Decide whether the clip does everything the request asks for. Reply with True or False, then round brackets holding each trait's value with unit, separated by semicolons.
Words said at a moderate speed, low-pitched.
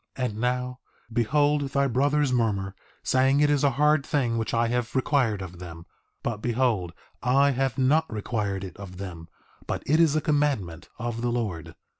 True (180 wpm; 125 Hz)